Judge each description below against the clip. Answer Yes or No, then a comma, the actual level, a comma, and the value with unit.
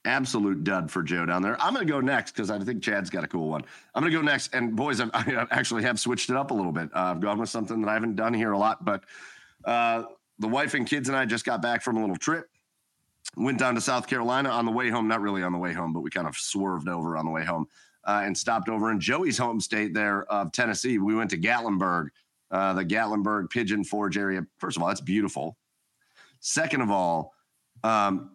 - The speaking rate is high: Yes, fast, 250 wpm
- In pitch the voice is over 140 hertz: No, low, 105 Hz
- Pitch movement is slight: No, average, 3.5 semitones